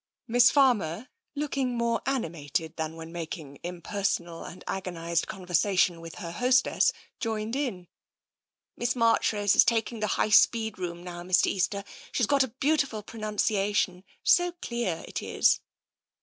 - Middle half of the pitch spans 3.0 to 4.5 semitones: No, wide, 5.6 semitones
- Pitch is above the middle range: Yes, high, 205 Hz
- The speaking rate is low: No, average, 150 wpm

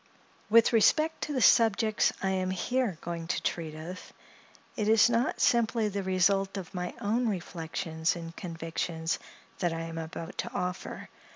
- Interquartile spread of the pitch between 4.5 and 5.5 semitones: Yes, average, 5.0 semitones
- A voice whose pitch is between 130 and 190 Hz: Yes, medium, 185 Hz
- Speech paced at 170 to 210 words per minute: No, average, 160 wpm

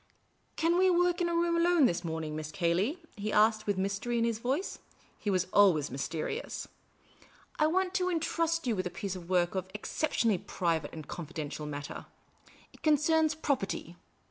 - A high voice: Yes, high, 210 Hz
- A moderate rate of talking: Yes, average, 195 wpm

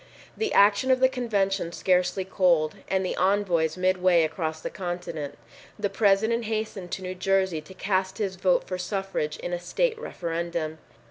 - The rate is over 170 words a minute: No, average, 165 wpm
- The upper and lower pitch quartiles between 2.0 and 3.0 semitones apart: Yes, narrow, 2.6 semitones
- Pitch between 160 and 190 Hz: Yes, medium, 185 Hz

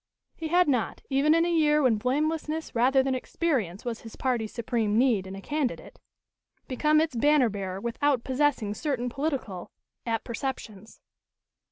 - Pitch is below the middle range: No, very high, 260 Hz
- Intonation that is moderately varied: Yes, average, 5.0 semitones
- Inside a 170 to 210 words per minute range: No, average, 150 wpm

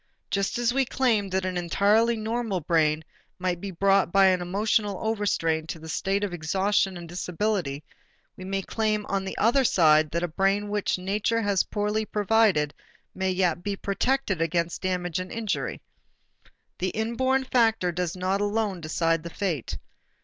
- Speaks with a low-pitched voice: No, high, 195 Hz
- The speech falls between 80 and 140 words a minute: No, average, 165 wpm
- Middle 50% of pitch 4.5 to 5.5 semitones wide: No, average, 3.3 semitones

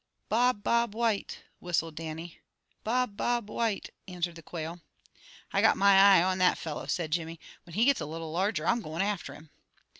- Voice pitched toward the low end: No, medium, 185 Hz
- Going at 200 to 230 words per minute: No, average, 180 wpm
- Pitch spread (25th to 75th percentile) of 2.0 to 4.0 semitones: No, average, 4.7 semitones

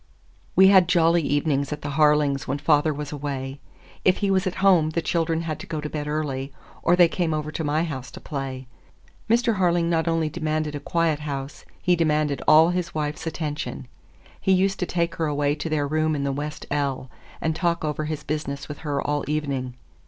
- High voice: No, medium, 155 Hz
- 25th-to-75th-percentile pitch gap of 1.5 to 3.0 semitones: Yes, narrow, 2.4 semitones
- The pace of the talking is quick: Yes, fast, 210 wpm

